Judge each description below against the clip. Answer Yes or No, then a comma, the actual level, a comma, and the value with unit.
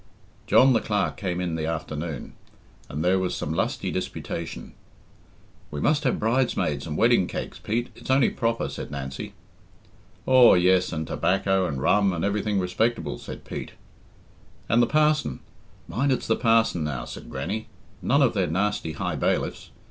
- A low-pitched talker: Yes, very low, 95 Hz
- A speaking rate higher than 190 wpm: No, average, 160 wpm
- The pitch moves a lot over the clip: Yes, wide, 6.4 semitones